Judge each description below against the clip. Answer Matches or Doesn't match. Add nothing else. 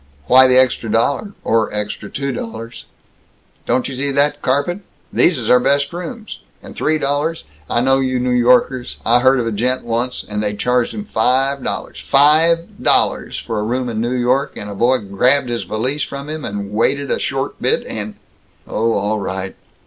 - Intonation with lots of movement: Doesn't match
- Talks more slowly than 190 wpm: Doesn't match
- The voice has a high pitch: Doesn't match